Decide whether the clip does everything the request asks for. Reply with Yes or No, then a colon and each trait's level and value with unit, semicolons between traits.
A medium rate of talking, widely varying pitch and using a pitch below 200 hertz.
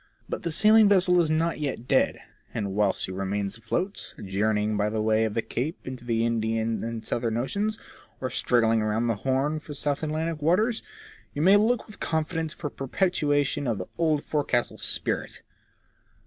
Yes: average, 170 wpm; wide, 6.6 semitones; low, 135 Hz